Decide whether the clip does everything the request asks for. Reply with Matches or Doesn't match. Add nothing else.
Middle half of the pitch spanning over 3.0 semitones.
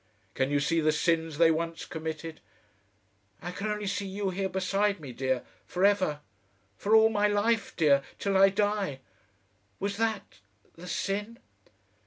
Matches